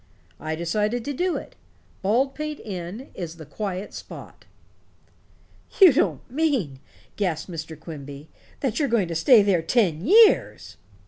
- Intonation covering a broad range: Yes, wide, 8.3 semitones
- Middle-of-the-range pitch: No, high, 200 Hz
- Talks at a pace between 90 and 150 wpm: Yes, slow, 135 wpm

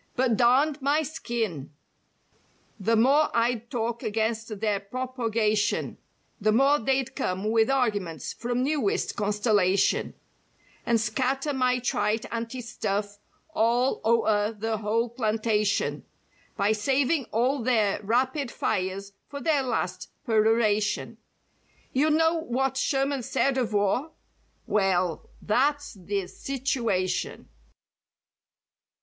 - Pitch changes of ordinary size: Yes, average, 3.9 semitones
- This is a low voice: No, high, 230 Hz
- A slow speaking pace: Yes, slow, 110 wpm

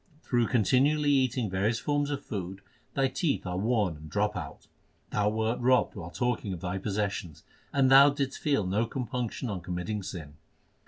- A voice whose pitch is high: No, low, 110 Hz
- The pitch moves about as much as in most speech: No, wide, 5.7 semitones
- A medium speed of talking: Yes, average, 170 wpm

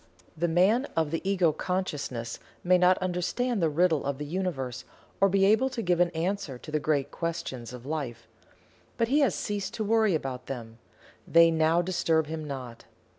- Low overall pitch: No, medium, 165 Hz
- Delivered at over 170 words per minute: Yes, average, 180 wpm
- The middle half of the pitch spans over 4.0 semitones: Yes, average, 4.8 semitones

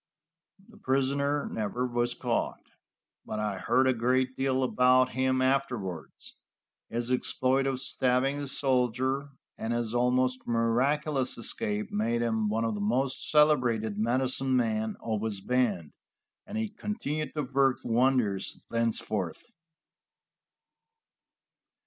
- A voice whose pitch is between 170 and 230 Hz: No, low, 125 Hz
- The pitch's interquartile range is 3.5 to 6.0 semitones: No, average, 2.8 semitones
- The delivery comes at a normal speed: No, slow, 120 wpm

